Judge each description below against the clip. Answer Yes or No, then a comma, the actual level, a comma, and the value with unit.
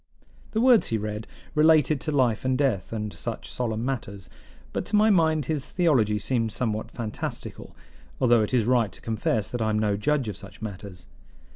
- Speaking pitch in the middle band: No, low, 115 Hz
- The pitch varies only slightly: No, average, 5.3 semitones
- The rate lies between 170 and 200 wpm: Yes, average, 185 wpm